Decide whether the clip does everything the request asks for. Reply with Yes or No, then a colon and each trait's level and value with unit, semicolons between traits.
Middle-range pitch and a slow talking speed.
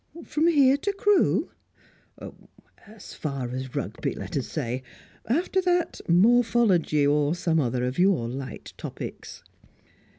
Yes: medium, 175 Hz; slow, 125 wpm